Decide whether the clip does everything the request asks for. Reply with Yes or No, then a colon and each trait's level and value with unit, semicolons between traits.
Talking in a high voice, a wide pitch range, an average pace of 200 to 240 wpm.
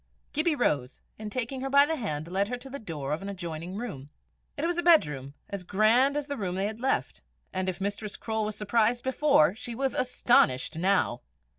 Yes: high, 215 Hz; wide, 6.6 semitones; fast, 205 wpm